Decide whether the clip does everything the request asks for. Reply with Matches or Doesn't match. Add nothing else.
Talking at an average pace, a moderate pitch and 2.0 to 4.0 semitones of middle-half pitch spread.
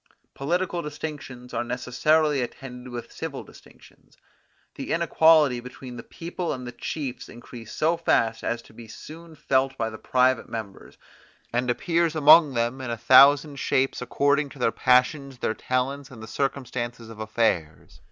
Doesn't match